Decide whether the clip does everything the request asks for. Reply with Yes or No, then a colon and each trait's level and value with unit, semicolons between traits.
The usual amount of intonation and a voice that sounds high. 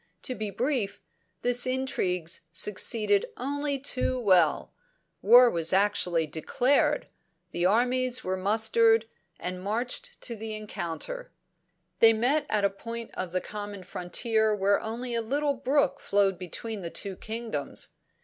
Yes: average, 4.6 semitones; high, 220 Hz